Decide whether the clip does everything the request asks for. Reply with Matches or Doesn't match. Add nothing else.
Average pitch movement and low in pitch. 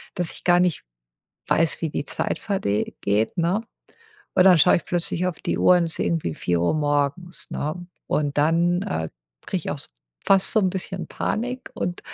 Doesn't match